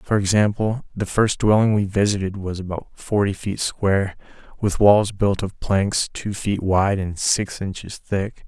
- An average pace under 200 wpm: Yes, average, 170 wpm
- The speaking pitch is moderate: No, low, 100 Hz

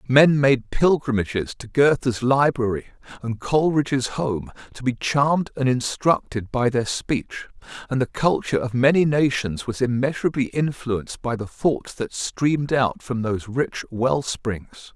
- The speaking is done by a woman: No, male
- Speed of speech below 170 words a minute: Yes, average, 150 wpm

